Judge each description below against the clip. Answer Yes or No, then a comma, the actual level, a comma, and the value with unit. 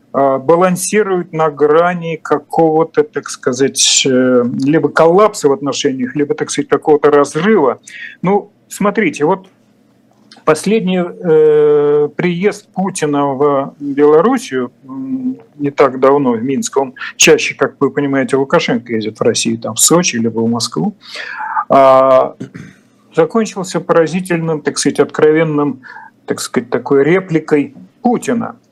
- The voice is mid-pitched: Yes, medium, 155 Hz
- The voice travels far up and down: No, average, 4.8 semitones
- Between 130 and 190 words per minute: No, average, 115 wpm